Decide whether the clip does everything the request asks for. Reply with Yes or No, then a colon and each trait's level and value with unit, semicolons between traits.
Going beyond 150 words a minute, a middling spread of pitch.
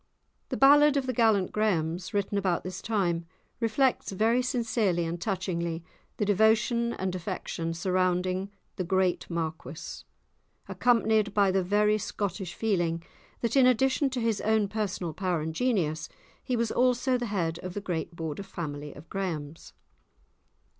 No: average, 145 wpm; average, 4.6 semitones